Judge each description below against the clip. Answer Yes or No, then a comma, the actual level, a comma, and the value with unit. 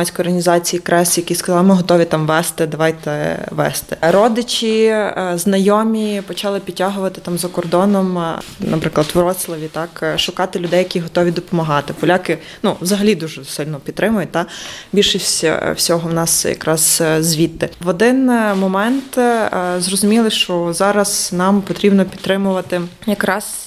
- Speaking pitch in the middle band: Yes, medium, 180 Hz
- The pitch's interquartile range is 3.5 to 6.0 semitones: No, average, 2.8 semitones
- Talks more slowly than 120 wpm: No, average, 130 wpm